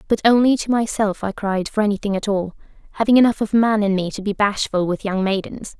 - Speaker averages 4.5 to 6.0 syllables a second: Yes, 5.8 syllables/s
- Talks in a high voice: Yes, high, 205 Hz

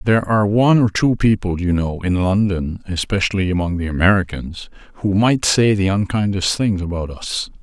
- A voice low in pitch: Yes, low, 100 Hz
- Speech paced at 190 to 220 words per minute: No, average, 175 wpm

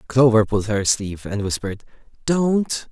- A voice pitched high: No, low, 115 Hz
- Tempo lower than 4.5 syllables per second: No, 5.2 syllables/s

